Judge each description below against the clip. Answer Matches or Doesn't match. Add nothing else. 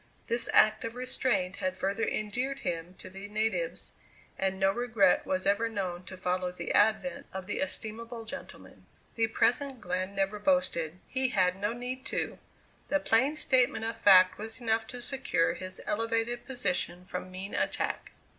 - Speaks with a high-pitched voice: Matches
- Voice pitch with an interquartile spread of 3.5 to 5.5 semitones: Matches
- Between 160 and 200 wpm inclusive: Matches